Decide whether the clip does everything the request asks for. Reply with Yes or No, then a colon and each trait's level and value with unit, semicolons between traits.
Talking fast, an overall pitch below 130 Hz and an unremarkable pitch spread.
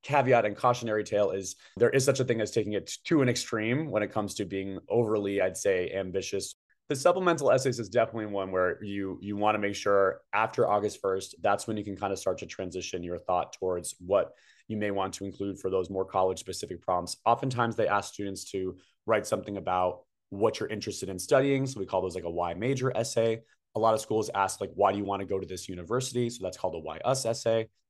Yes: fast, 230 wpm; low, 100 Hz; average, 3.1 semitones